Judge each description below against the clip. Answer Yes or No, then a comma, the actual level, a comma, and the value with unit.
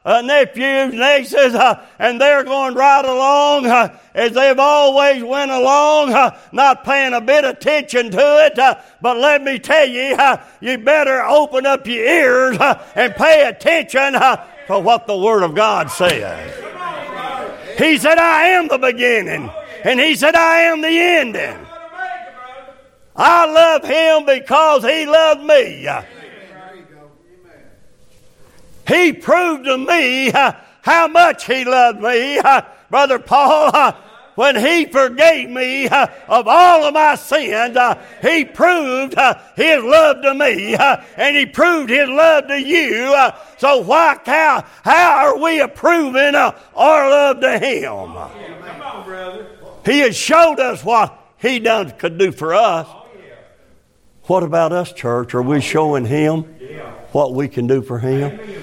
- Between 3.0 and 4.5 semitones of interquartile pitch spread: Yes, average, 3.9 semitones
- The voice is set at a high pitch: Yes, very high, 275 Hz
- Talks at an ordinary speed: Yes, average, 150 wpm